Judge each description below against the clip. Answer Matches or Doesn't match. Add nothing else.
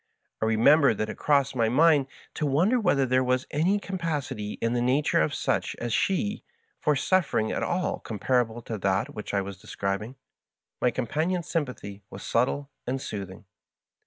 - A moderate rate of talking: Matches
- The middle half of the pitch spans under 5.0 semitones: Doesn't match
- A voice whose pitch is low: Matches